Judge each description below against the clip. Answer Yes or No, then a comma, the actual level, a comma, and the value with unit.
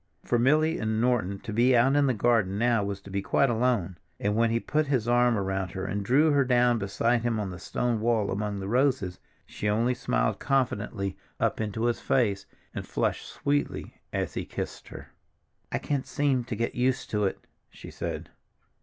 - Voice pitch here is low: Yes, low, 115 Hz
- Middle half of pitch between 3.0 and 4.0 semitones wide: Yes, average, 3.7 semitones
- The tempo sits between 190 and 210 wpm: Yes, average, 200 wpm